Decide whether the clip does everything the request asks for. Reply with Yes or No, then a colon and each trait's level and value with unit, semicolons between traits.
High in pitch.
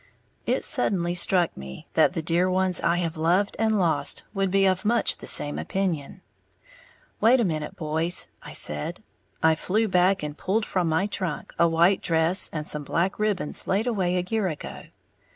No: medium, 180 Hz